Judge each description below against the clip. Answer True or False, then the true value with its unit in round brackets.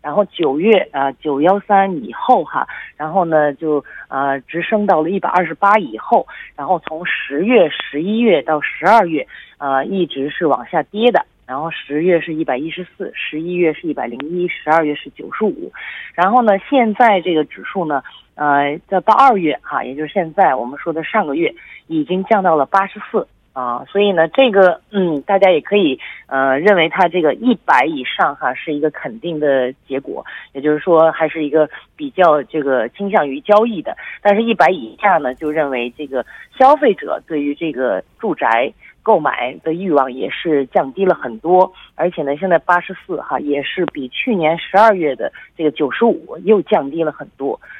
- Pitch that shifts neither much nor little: True (4.9 semitones)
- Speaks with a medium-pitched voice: True (165 Hz)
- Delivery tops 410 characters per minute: False (275 characters per minute)